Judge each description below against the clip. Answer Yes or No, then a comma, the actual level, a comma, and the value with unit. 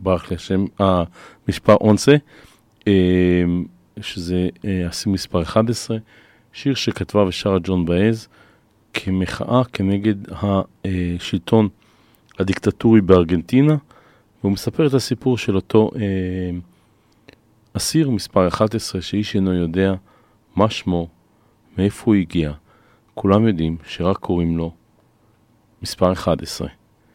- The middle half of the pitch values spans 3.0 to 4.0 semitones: Yes, average, 3.4 semitones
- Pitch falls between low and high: No, low, 100 Hz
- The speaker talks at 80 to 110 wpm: Yes, slow, 100 wpm